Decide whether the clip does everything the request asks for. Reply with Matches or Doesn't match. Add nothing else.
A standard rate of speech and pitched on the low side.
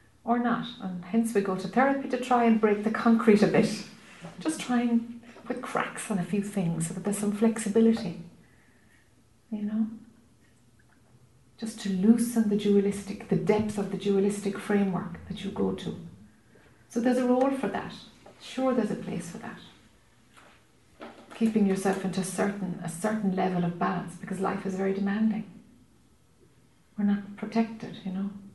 Doesn't match